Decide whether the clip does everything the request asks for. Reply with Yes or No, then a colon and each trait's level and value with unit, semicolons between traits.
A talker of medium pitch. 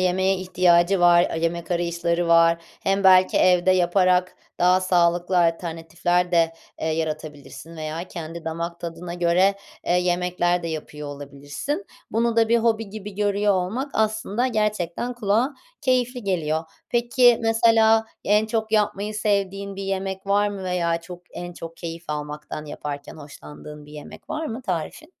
Yes: medium, 180 Hz